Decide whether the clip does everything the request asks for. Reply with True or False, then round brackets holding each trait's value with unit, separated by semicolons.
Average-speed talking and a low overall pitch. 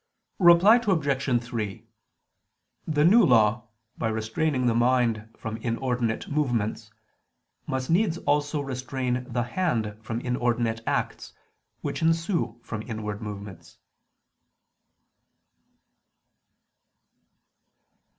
False (90 wpm; 125 Hz)